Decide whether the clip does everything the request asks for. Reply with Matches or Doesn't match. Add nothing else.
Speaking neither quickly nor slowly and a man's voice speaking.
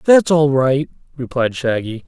Matches